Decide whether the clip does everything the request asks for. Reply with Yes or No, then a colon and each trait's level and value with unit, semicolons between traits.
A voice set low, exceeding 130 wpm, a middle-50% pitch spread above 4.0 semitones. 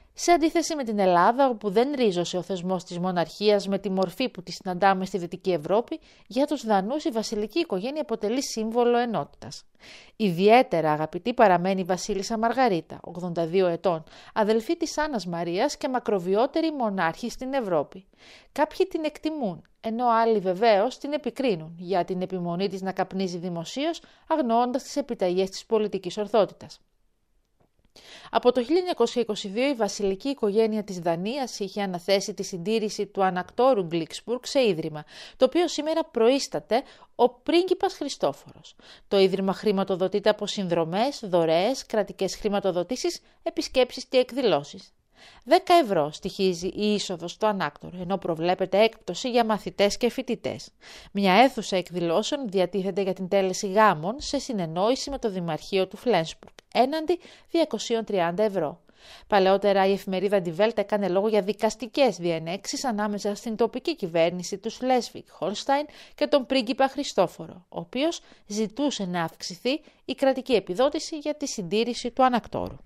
No: high, 210 Hz; average, 140 wpm; average, 5.2 semitones